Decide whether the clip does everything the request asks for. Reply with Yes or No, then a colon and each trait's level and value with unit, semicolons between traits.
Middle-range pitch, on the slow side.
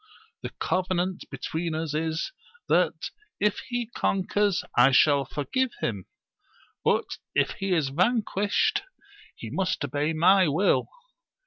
Yes: medium, 180 Hz; slow, 120 wpm